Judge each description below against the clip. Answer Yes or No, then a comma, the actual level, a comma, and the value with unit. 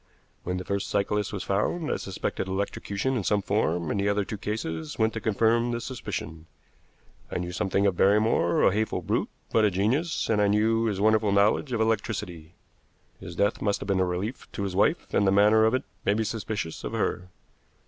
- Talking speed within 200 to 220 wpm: Yes, fast, 205 wpm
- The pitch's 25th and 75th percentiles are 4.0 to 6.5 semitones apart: No, narrow, 2.4 semitones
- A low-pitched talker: Yes, low, 100 Hz